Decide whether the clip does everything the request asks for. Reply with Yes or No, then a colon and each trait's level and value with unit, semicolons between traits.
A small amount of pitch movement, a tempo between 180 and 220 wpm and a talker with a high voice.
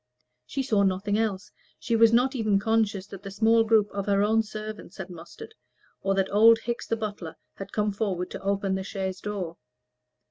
Yes: narrow, 2.3 semitones; average, 190 wpm; high, 205 Hz